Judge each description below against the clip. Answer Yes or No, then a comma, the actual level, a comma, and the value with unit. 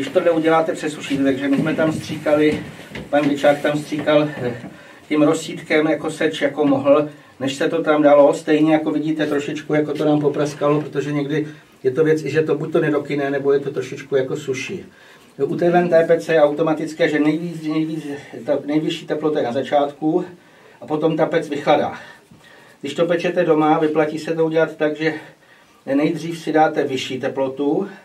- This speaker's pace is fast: Yes, fast, 180 wpm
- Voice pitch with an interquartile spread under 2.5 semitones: Yes, narrow, 1.8 semitones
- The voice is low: No, medium, 155 Hz